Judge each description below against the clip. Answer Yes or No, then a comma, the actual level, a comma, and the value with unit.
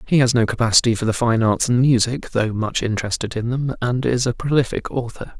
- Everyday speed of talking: No, fast, 220 wpm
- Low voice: Yes, low, 120 Hz